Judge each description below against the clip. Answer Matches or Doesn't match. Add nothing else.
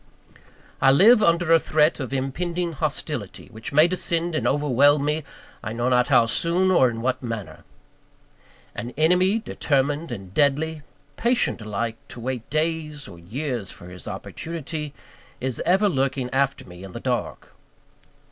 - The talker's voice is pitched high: Doesn't match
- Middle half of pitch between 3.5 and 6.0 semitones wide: Matches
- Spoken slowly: Doesn't match